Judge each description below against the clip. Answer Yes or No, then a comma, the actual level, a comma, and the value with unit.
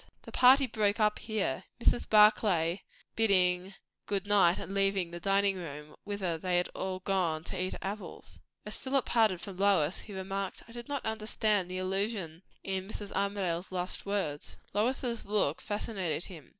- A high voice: Yes, high, 195 Hz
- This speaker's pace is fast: No, average, 165 wpm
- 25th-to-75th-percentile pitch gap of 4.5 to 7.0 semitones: No, average, 2.8 semitones